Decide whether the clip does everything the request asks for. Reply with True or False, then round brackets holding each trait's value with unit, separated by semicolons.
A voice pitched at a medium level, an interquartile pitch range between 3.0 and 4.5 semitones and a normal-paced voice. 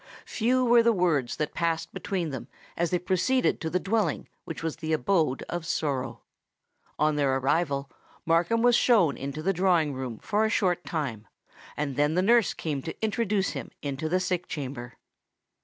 False (165 Hz; 5.3 semitones; 175 wpm)